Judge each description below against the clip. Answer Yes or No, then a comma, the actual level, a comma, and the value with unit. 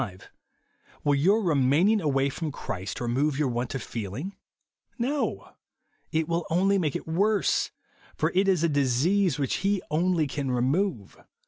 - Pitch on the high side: No, medium, 155 Hz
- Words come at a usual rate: Yes, average, 145 wpm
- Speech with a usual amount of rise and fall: No, wide, 5.8 semitones